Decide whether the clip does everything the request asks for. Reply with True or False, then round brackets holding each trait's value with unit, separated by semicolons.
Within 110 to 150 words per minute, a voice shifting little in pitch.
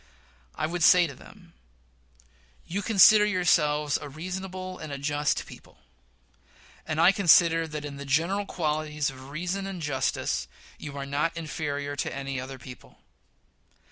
False (145 wpm; 4.1 semitones)